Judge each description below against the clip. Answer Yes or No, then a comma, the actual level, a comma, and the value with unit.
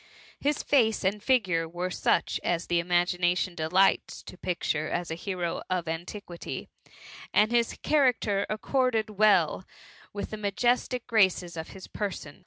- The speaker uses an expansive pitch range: No, average, 3.8 semitones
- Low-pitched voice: No, high, 190 Hz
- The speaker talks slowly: No, average, 145 wpm